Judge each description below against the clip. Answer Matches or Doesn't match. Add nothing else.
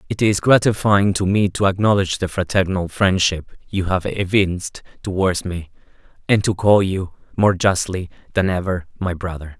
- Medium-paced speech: Matches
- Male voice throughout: Matches